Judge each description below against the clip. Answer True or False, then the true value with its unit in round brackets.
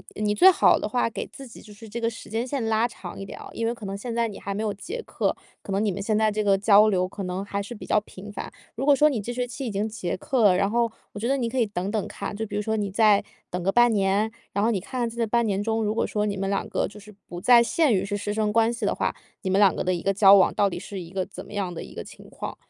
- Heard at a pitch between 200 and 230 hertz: True (210 Hz)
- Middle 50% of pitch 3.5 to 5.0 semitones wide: False (2.8 semitones)